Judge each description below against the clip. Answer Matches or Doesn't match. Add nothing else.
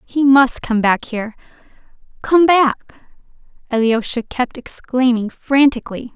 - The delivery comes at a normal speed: Doesn't match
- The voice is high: Matches